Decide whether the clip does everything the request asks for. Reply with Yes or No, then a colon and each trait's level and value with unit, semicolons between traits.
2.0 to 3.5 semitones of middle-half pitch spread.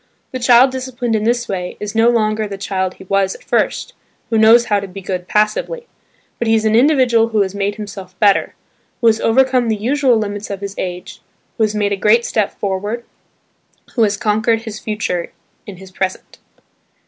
Yes: average, 2.9 semitones